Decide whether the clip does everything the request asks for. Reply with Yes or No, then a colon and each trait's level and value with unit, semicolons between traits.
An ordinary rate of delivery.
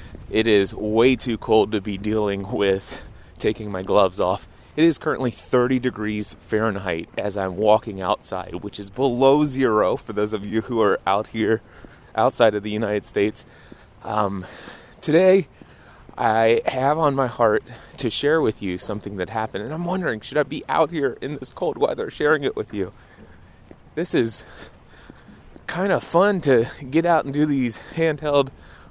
Yes: average, 170 wpm